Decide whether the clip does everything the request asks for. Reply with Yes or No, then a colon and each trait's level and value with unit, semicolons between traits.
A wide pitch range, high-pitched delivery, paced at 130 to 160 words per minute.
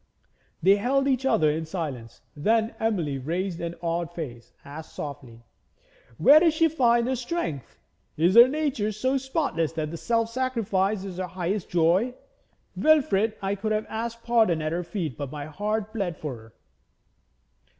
Yes: wide, 6.6 semitones; high, 195 Hz; average, 155 wpm